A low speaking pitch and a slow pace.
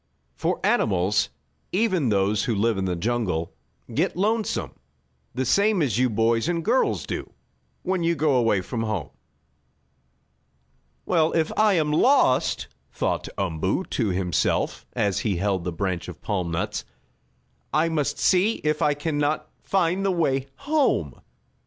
No: low, 130 Hz; average, 145 wpm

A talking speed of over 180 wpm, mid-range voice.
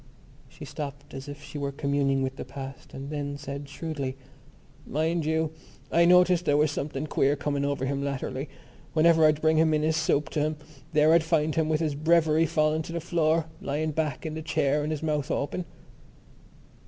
Yes: average, 190 wpm; medium, 150 Hz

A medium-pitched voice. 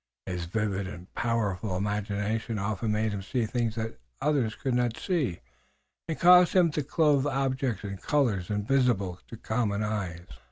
No: low, 110 Hz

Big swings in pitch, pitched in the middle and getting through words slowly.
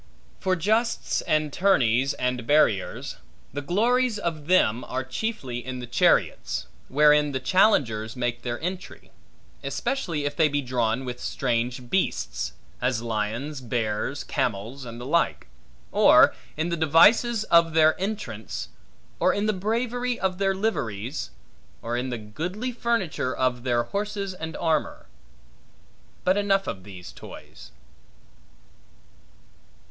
Yes: wide, 7.9 semitones; medium, 145 Hz; slow, 130 wpm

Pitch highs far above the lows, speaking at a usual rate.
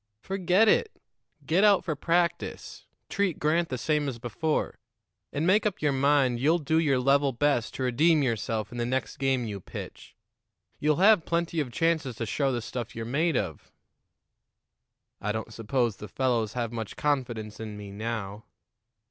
Yes: wide, 5.7 semitones; average, 170 wpm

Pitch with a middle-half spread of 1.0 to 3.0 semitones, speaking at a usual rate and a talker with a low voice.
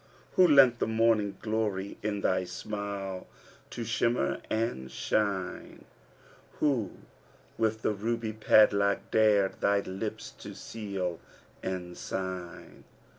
No: average, 2.7 semitones; slow, 115 wpm; low, 105 Hz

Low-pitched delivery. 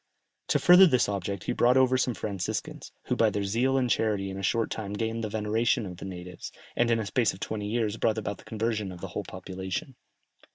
Yes: low, 110 Hz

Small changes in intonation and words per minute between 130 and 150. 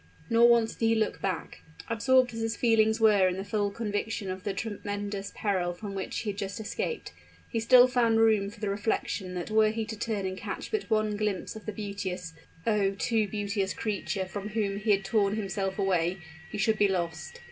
No: narrow, 2.2 semitones; fast, 205 wpm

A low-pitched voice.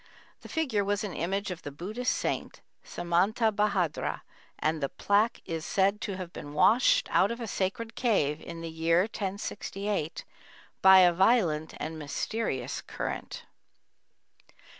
No: high, 190 Hz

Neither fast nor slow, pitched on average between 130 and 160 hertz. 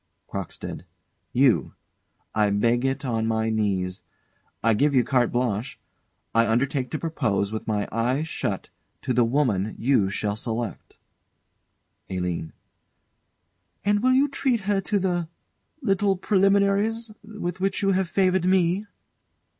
No: slow, 130 wpm; low, 135 Hz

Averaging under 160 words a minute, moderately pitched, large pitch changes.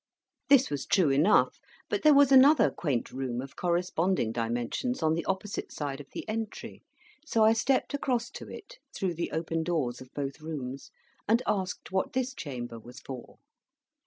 No: average, 170 wpm; medium, 170 Hz; wide, 8.9 semitones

